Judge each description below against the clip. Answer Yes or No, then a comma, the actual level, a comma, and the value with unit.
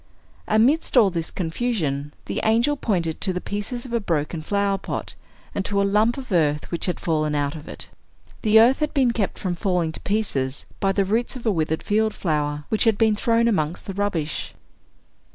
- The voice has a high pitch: Yes, high, 200 Hz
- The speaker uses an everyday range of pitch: No, wide, 5.7 semitones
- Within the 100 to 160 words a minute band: No, average, 200 wpm